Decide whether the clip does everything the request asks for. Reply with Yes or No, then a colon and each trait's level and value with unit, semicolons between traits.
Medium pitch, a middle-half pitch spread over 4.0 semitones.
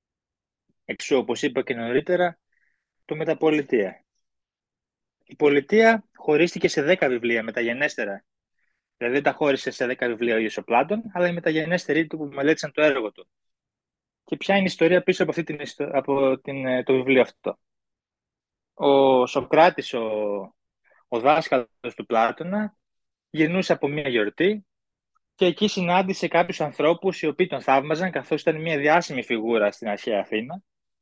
Yes: medium, 150 Hz; average, 5.2 semitones